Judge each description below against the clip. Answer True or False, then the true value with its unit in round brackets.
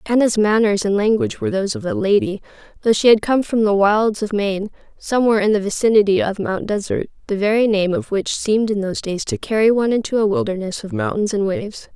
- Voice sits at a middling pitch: False (210 Hz)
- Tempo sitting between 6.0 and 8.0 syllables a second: True (6.3 syllables/s)